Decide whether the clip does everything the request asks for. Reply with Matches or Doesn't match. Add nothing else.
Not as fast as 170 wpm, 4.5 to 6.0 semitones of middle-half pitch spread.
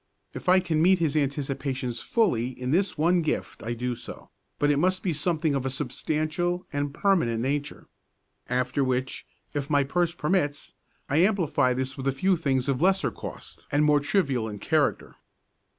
Doesn't match